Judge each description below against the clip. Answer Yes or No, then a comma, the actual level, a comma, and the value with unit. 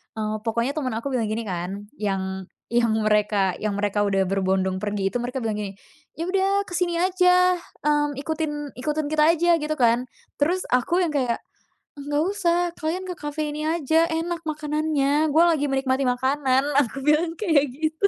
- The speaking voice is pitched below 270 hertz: No, very high, 290 Hz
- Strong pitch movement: Yes, wide, 6.3 semitones